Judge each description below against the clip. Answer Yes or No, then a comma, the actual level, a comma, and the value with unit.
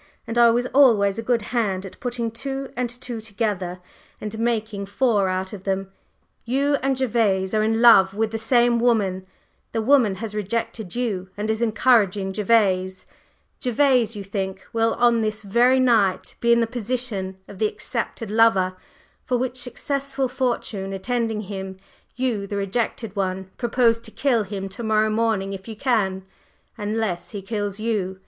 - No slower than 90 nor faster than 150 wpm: No, average, 165 wpm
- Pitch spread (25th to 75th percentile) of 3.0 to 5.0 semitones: Yes, average, 3.4 semitones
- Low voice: No, high, 220 Hz